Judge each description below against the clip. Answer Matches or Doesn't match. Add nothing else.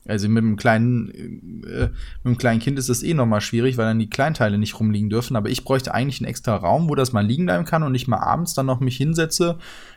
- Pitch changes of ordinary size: Matches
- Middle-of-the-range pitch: Doesn't match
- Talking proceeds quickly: Matches